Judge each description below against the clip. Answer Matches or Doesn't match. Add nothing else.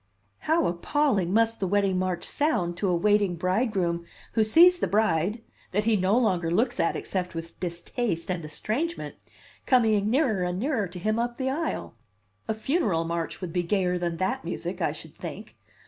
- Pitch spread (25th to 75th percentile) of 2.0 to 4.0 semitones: Doesn't match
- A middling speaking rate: Matches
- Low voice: Doesn't match